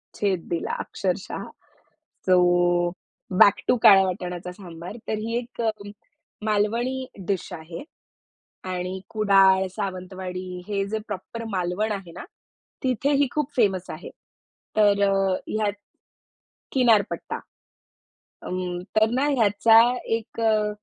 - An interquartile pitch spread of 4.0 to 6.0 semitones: No, average, 3.4 semitones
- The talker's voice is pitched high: Yes, high, 200 Hz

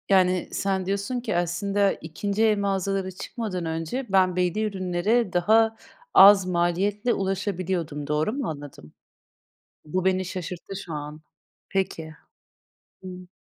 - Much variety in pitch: No, narrow, 2.5 semitones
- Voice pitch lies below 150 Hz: No, medium, 185 Hz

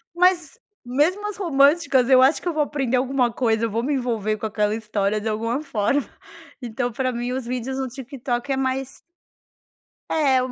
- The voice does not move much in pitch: No, average, 3.4 semitones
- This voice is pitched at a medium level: No, very high, 255 Hz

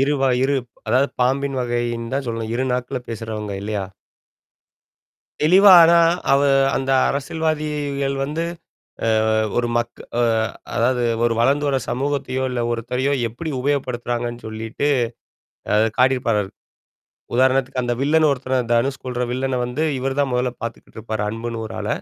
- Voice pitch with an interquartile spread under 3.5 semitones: Yes, average, 2.8 semitones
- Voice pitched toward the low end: Yes, low, 125 Hz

